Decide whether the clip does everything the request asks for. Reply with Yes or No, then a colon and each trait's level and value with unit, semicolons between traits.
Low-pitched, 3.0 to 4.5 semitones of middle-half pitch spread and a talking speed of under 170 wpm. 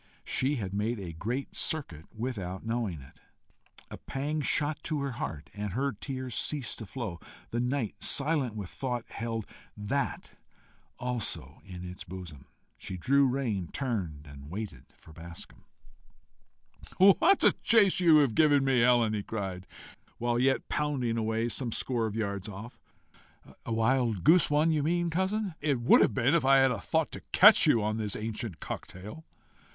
No: low, 120 Hz; wide, 5.5 semitones; average, 160 wpm